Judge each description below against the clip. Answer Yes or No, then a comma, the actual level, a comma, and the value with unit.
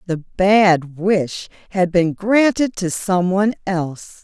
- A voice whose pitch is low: No, medium, 185 Hz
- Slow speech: Yes, slow, 125 wpm